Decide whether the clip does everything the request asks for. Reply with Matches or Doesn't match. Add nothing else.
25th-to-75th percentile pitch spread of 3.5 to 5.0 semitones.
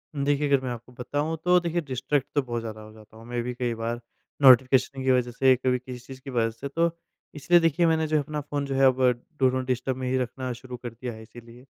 Doesn't match